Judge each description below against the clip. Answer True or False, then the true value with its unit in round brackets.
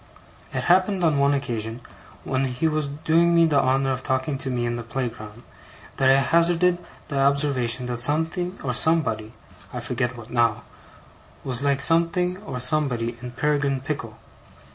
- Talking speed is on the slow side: False (165 wpm)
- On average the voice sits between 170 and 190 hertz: False (135 Hz)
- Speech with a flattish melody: False (4.5 semitones)